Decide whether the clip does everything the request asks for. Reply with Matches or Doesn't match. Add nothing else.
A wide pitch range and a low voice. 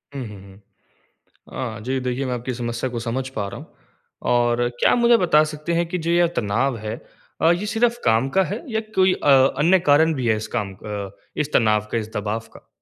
Matches